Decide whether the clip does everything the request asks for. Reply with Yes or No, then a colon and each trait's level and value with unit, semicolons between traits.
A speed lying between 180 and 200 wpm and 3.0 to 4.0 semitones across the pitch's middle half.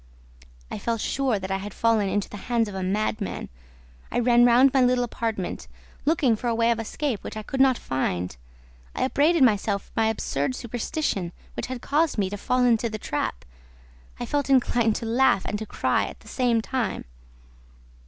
Yes: average, 195 wpm; average, 3.5 semitones